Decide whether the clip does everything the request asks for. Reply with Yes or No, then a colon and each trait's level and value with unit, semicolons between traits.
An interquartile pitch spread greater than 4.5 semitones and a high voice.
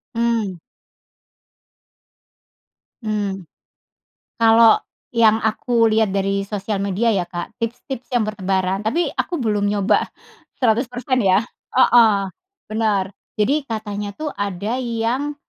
No: average, 2.9 semitones; high, 220 Hz